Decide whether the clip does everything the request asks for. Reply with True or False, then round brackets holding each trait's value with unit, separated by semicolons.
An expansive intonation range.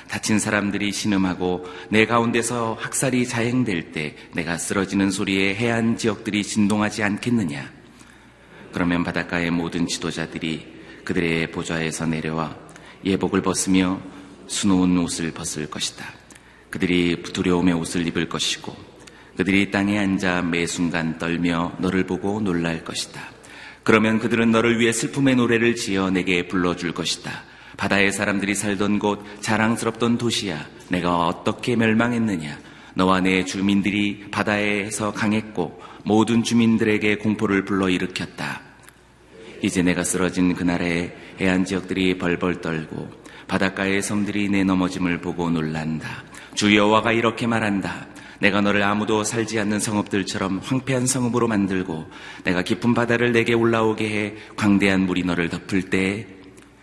False (3.3 semitones)